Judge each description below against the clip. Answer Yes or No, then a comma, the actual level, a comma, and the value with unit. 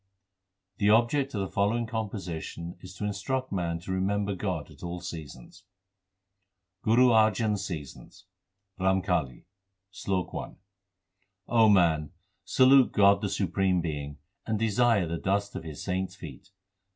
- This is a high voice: No, very low, 95 Hz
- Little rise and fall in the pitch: No, average, 3.9 semitones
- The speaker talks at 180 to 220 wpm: No, average, 140 wpm